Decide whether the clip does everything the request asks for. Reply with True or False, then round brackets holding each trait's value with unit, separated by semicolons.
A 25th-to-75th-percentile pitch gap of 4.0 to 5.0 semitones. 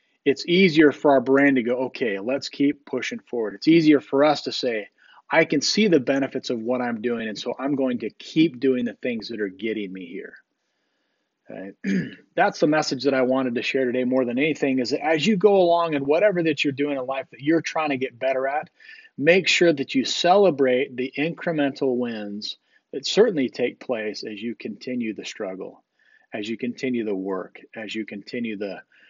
True (4.4 semitones)